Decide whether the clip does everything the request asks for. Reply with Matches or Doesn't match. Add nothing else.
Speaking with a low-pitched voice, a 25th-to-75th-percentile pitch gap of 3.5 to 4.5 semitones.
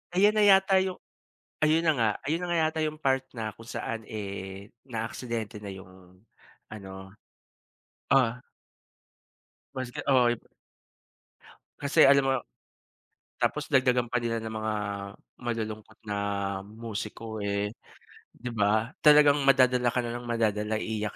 Matches